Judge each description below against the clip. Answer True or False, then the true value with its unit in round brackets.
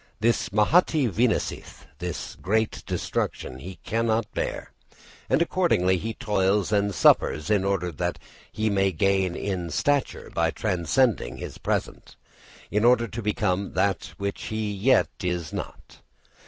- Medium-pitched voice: False (100 Hz)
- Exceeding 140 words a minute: False (135 wpm)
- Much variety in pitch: False (3.7 semitones)